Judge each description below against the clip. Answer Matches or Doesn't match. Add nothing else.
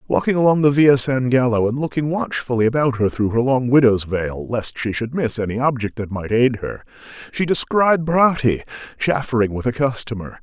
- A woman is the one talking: Doesn't match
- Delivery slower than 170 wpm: Doesn't match